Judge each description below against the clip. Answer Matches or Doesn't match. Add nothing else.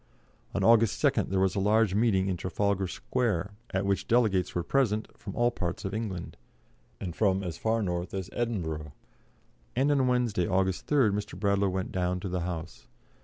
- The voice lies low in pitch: Matches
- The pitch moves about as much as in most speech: Matches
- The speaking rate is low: Doesn't match